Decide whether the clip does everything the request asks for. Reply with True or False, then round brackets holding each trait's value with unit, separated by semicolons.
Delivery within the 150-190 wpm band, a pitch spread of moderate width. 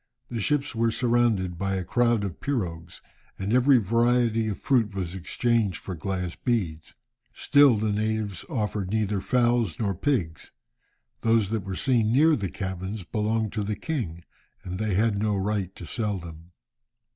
True (160 wpm; 3.7 semitones)